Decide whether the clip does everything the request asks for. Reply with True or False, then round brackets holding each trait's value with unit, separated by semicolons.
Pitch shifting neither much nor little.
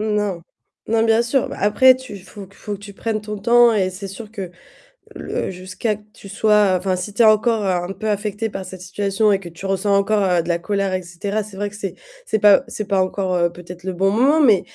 False (2.3 semitones)